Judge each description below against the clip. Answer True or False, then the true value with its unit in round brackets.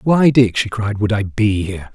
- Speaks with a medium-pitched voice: False (110 Hz)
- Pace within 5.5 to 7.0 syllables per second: False (4.9 syllables/s)